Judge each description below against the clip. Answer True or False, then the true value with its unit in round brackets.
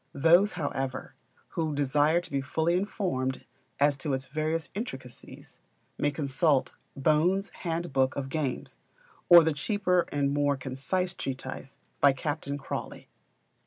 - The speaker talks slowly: True (125 wpm)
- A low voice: False (145 Hz)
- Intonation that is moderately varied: True (3.9 semitones)